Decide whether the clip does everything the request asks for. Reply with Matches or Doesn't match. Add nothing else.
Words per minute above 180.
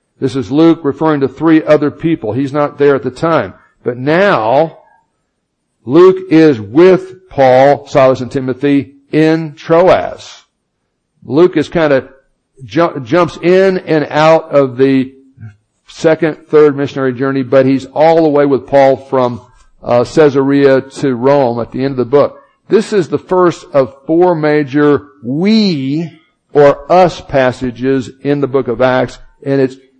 Doesn't match